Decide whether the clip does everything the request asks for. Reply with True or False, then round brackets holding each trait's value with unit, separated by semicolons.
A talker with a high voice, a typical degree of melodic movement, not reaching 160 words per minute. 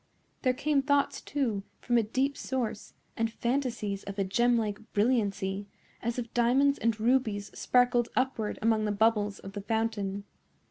True (230 Hz; 3.4 semitones; 150 wpm)